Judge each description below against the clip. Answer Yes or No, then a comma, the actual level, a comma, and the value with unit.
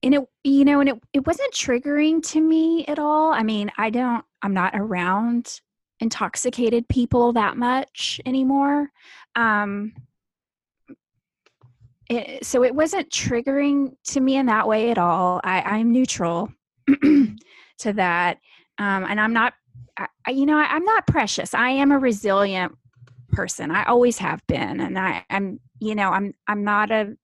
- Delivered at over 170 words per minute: No, average, 160 wpm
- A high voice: Yes, high, 235 Hz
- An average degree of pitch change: No, wide, 5.7 semitones